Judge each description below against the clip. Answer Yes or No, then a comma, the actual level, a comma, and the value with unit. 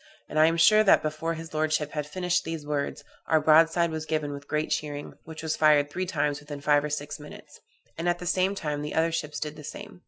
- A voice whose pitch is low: No, medium, 155 Hz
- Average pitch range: No, narrow, 1.8 semitones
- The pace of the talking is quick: Yes, fast, 245 wpm